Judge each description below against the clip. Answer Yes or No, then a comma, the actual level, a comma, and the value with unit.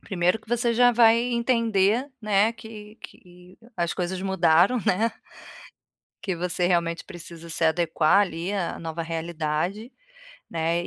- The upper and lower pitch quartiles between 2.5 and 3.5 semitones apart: No, average, 4.6 semitones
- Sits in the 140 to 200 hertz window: Yes, medium, 185 Hz